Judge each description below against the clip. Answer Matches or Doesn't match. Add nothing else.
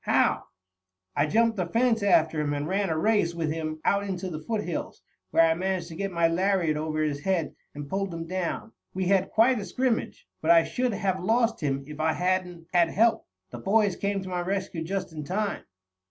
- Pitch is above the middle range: Doesn't match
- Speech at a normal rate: Doesn't match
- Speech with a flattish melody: Doesn't match